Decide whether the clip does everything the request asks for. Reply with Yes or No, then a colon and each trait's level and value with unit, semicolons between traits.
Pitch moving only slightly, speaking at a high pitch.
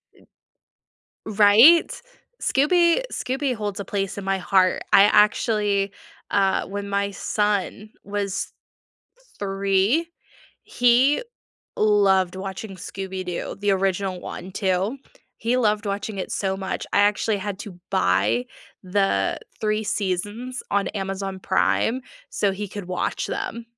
Yes: narrow, 1.9 semitones; high, 200 Hz